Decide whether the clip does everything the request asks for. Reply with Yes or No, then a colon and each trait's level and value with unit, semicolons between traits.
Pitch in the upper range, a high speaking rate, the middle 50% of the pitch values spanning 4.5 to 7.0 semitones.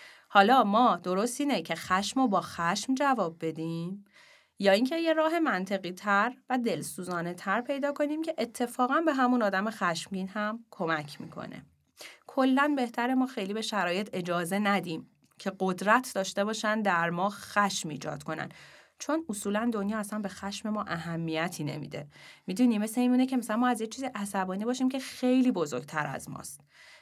Yes: high, 205 Hz; fast, 160 wpm; wide, 5.5 semitones